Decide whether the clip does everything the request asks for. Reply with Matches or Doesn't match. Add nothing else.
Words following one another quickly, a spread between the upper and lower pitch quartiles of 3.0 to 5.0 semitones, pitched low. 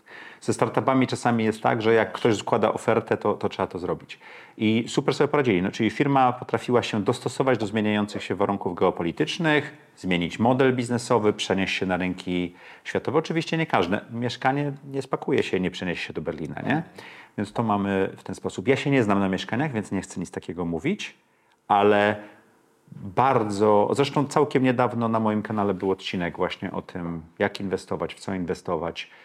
Matches